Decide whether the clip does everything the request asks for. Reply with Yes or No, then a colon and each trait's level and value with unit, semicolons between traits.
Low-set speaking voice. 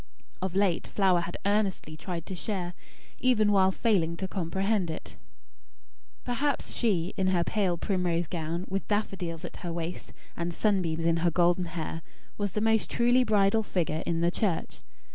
No: medium, 185 Hz